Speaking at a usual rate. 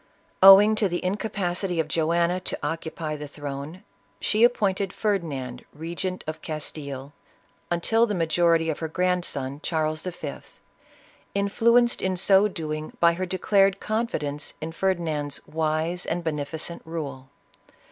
No: slow, 130 wpm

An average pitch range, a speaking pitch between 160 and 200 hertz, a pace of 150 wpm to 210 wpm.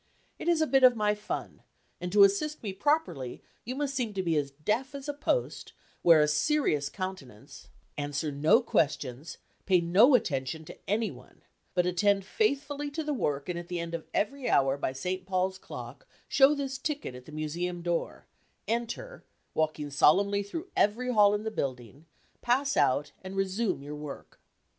No: wide, 8.8 semitones; high, 190 Hz; average, 180 wpm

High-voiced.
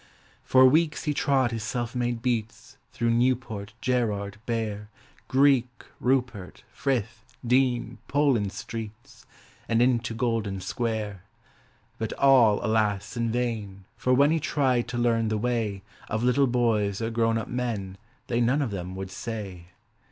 No: low, 115 Hz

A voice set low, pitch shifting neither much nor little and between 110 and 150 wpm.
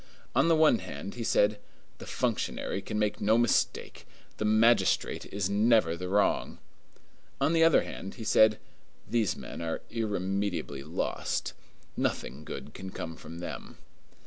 Yes: low, 105 Hz; average, 3.7 semitones; average, 145 wpm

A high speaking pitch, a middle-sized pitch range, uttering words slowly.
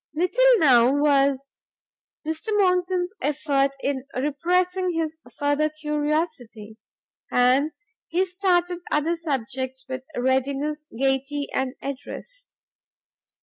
Yes: very high, 295 Hz; average, 4.4 semitones; slow, 95 wpm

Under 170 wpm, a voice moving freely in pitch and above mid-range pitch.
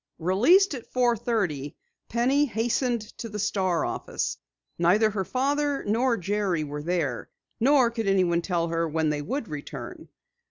Yes: average, 150 wpm; wide, 6.2 semitones; high, 210 Hz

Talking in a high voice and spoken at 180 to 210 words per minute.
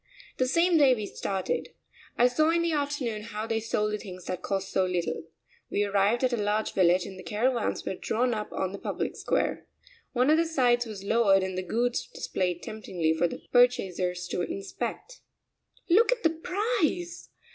Yes: high, 220 Hz; average, 190 wpm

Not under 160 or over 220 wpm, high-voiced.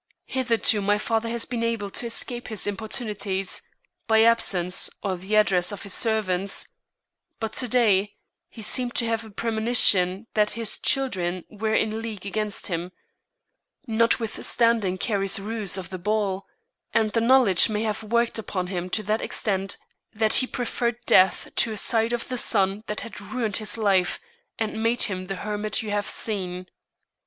Yes: average, 165 wpm; high, 215 Hz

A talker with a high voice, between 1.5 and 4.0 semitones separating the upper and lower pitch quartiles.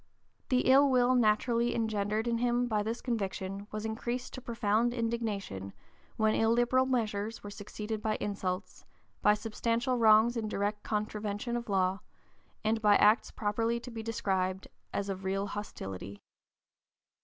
Yes: high, 220 Hz; narrow, 2.5 semitones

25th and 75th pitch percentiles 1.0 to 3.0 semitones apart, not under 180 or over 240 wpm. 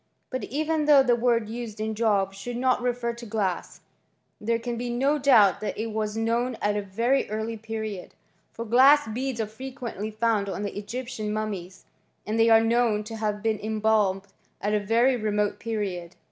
No: narrow, 2.4 semitones; average, 170 wpm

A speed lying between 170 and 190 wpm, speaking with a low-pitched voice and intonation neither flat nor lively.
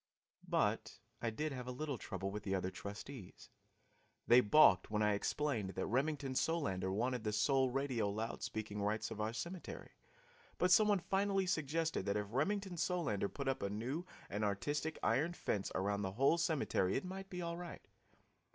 No: average, 180 wpm; low, 130 Hz; wide, 7.6 semitones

